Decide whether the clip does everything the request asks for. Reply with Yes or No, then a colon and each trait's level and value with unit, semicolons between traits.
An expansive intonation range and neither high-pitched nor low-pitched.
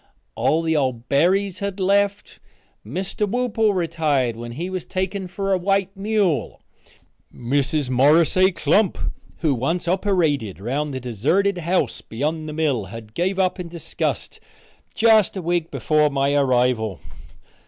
Yes: wide, 5.9 semitones; medium, 165 Hz